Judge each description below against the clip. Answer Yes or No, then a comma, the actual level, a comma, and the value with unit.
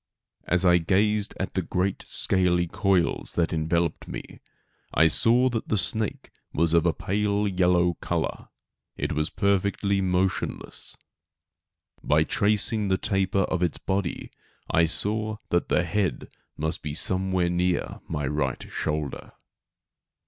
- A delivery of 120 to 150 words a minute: Yes, slow, 135 wpm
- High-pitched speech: No, very low, 90 Hz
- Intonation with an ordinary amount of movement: Yes, average, 3.0 semitones